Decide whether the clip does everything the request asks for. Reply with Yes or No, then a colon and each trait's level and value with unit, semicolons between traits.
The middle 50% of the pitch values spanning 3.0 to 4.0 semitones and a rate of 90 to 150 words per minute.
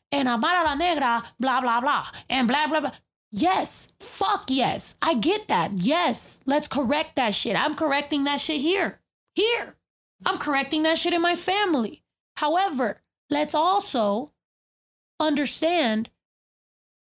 No: average, 5.1 semitones; slow, 135 wpm